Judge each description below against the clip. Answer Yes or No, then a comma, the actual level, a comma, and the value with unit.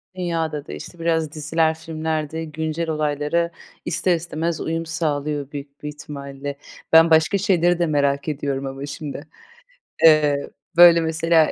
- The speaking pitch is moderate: Yes, medium, 160 Hz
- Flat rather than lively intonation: Yes, narrow, 2.2 semitones